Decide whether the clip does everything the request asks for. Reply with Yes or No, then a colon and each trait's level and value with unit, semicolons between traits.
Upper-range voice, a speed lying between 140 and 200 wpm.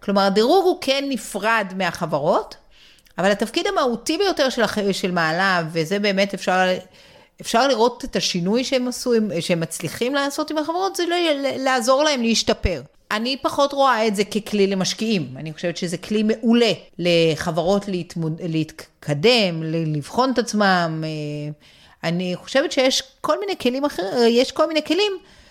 Yes: high, 215 Hz; average, 145 wpm